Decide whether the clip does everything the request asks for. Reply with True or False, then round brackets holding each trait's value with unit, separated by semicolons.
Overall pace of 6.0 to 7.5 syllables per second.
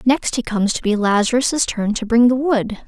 False (5.1 syllables/s)